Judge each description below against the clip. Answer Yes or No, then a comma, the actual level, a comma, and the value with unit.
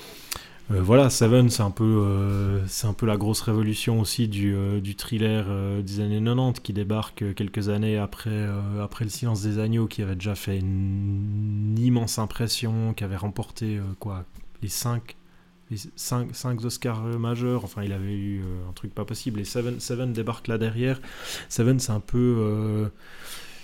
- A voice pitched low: Yes, low, 110 Hz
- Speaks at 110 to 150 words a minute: No, average, 175 wpm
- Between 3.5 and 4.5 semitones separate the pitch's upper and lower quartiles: No, narrow, 2.6 semitones